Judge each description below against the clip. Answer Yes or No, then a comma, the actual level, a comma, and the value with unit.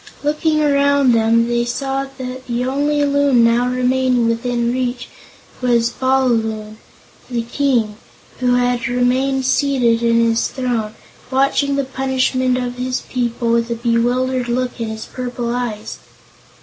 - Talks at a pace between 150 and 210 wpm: No, average, 140 wpm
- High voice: Yes, very high, 250 Hz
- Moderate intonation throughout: No, narrow, 2.0 semitones